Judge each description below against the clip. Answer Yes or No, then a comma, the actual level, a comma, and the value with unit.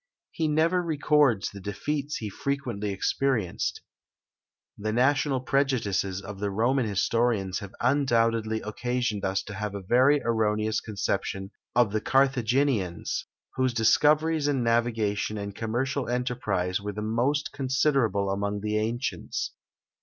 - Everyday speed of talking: No, slow, 125 wpm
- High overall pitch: No, low, 115 Hz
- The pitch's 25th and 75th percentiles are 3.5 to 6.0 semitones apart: Yes, average, 4.7 semitones